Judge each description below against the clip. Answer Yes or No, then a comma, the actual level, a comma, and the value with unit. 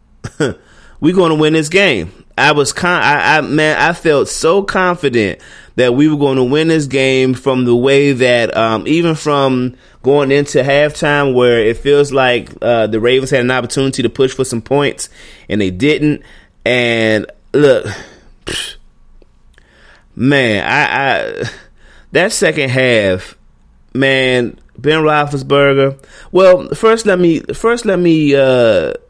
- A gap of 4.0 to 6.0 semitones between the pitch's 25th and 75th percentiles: No, average, 3.5 semitones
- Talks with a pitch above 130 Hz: Yes, medium, 140 Hz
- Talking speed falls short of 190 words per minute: Yes, average, 145 wpm